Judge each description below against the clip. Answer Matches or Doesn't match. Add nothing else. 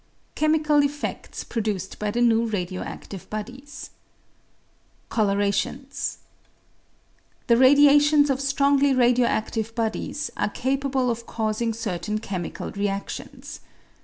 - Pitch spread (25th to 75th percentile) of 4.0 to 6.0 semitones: Matches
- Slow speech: Matches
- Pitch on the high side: Matches